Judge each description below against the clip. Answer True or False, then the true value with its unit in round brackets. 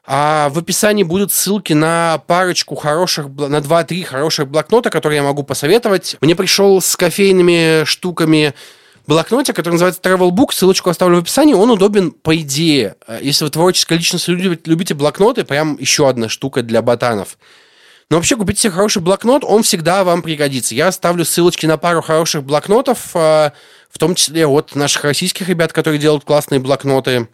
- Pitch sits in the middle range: True (165 Hz)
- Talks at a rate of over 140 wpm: True (160 wpm)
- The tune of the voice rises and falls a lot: False (3.9 semitones)